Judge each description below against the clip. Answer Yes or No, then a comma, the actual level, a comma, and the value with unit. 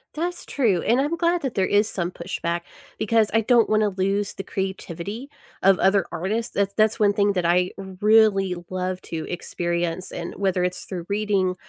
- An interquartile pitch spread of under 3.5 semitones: Yes, average, 2.9 semitones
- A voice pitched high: Yes, high, 195 Hz